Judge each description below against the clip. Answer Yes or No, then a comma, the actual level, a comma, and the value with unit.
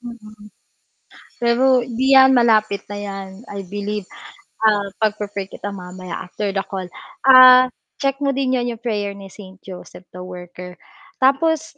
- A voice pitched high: Yes, high, 210 Hz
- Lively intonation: No, average, 4.6 semitones